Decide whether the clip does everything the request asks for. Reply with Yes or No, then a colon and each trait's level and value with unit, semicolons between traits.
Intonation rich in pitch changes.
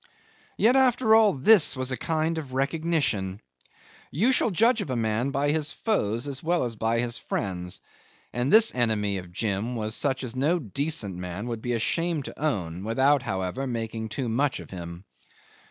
Yes: wide, 6.6 semitones